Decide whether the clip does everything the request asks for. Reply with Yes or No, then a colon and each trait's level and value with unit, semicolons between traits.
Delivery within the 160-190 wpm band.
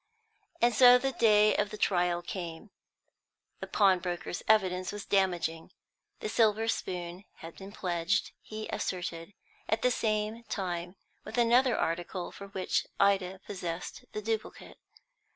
No: slow, 135 wpm